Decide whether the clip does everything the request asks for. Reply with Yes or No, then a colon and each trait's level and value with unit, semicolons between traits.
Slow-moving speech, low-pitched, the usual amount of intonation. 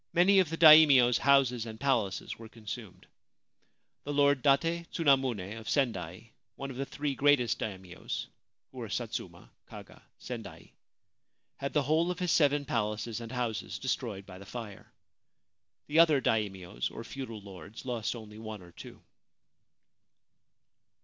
No: average, 145 wpm; low, 120 Hz; average, 4.9 semitones